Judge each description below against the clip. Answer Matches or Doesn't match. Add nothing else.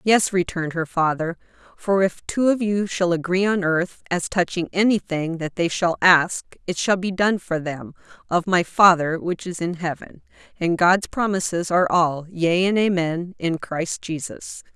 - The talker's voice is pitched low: Doesn't match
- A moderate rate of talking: Matches